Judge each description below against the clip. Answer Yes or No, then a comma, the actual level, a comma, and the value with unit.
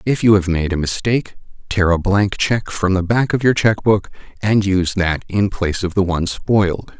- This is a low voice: Yes, low, 100 Hz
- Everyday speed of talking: No, fast, 225 wpm